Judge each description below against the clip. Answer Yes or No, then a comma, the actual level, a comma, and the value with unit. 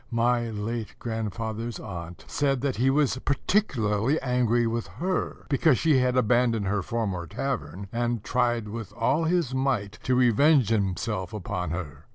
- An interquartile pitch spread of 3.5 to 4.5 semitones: Yes, average, 3.8 semitones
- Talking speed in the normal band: Yes, average, 150 wpm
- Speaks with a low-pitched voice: Yes, low, 115 Hz